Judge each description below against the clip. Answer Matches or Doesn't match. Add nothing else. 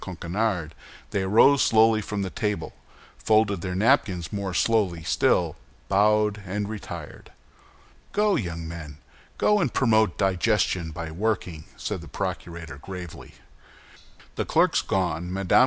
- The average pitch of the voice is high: Doesn't match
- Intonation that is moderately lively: Matches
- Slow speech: Matches